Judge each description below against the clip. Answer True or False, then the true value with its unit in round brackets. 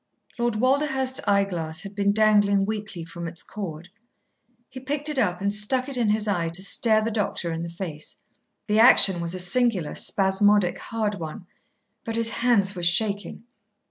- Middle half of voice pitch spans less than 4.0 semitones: False (4.3 semitones)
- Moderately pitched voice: False (205 Hz)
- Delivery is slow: False (175 wpm)